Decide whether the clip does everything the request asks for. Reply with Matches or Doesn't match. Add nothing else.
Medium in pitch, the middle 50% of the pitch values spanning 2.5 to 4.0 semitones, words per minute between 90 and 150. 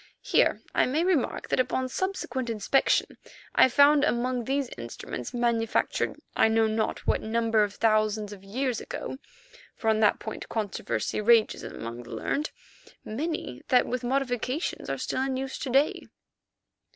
Doesn't match